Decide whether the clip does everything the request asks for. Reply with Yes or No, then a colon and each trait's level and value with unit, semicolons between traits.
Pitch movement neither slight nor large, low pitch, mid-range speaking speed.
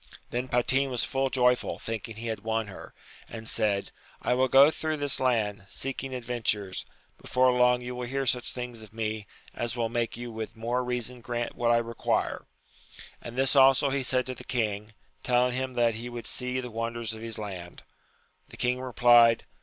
No: narrow, 2.0 semitones; low, 120 Hz; average, 190 wpm